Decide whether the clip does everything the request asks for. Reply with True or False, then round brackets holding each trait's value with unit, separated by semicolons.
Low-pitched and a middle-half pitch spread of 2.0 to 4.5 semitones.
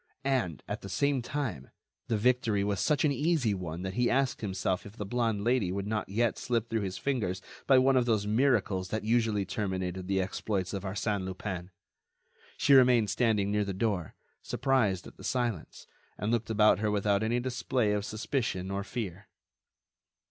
True (105 Hz; 3.9 semitones)